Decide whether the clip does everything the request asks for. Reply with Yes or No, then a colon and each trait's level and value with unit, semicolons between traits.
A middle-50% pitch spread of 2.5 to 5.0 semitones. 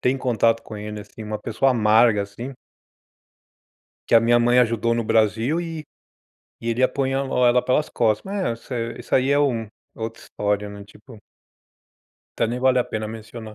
Yes: average, 2.9 semitones